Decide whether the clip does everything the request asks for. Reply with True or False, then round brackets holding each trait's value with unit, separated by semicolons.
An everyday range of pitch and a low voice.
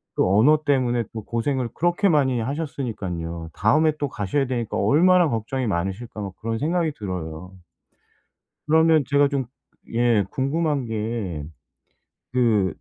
False (5.7 semitones; 120 Hz)